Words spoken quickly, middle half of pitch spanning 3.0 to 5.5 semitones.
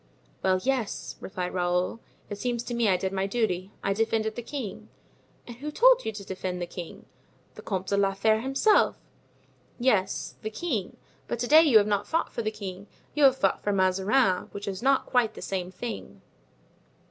No: average, 195 wpm; average, 4.2 semitones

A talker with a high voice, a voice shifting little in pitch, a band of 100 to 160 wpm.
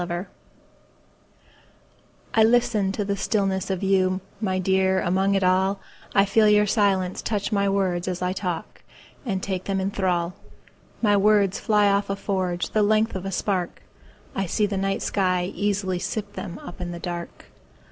Yes: high, 195 Hz; narrow, 1.7 semitones; average, 145 wpm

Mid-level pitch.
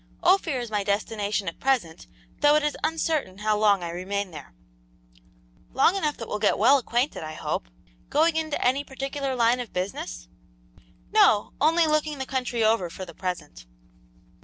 No: high, 235 Hz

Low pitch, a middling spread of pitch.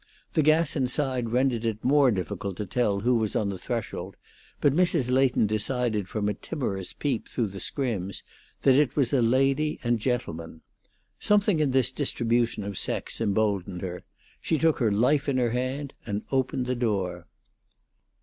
Yes: low, 120 Hz; average, 4.7 semitones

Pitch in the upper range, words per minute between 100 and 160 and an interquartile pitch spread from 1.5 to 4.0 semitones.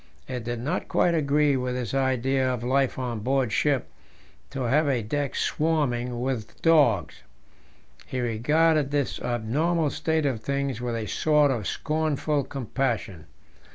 No: low, 135 Hz; average, 145 wpm; average, 3.5 semitones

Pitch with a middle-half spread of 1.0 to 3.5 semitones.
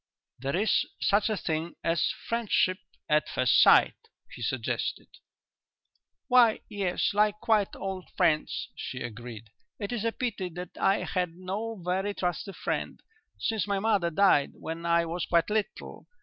No: average, 3.9 semitones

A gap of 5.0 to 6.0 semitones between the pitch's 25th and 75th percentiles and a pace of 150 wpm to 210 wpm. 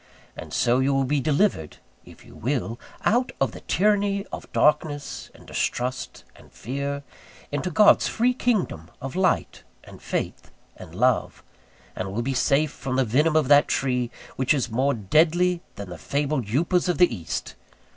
Yes: wide, 5.5 semitones; average, 165 wpm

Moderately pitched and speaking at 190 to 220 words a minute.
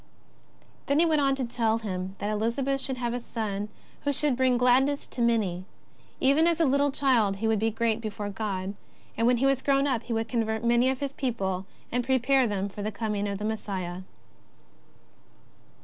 No: high, 235 Hz; average, 195 wpm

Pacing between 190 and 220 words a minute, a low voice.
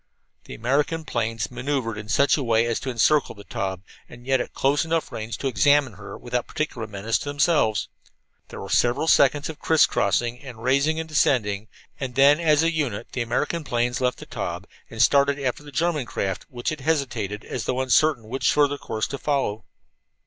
Yes: average, 195 wpm; low, 130 Hz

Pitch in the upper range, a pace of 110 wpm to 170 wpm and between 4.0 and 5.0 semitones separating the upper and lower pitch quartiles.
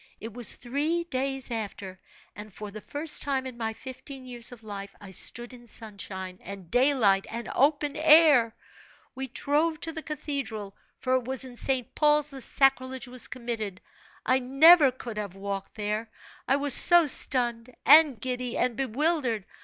Yes: very high, 250 Hz; average, 165 wpm; average, 4.3 semitones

